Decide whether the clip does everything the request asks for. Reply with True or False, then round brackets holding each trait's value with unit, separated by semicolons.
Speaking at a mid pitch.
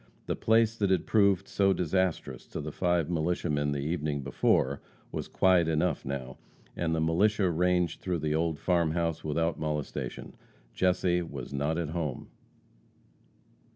False (85 Hz)